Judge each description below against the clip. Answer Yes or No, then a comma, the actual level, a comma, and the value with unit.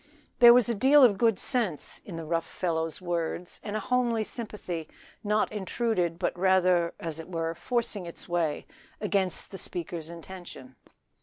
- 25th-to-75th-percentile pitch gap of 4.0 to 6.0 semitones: Yes, average, 4.4 semitones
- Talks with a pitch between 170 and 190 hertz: Yes, medium, 185 Hz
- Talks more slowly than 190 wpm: Yes, average, 160 wpm